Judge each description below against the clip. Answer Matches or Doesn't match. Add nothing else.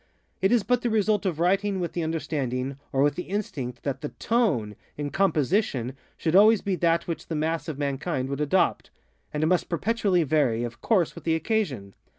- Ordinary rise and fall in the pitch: Doesn't match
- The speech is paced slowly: Doesn't match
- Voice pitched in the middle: Matches